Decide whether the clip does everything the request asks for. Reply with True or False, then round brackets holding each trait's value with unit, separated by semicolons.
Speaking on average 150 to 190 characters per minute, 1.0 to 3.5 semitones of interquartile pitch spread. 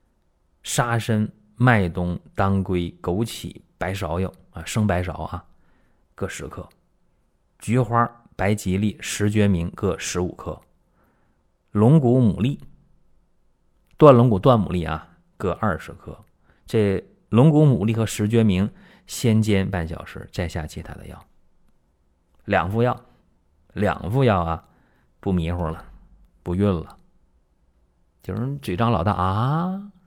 False (175 characters per minute; 5.1 semitones)